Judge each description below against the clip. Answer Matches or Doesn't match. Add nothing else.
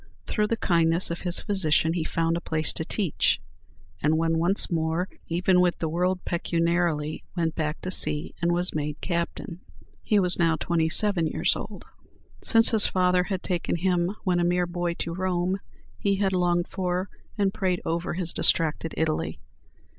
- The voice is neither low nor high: Matches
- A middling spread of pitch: Doesn't match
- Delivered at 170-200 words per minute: Matches